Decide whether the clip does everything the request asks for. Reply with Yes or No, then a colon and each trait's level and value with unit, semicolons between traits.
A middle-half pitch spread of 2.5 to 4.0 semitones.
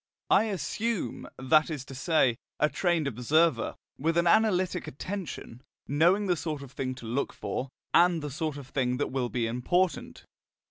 No: average, 5.1 semitones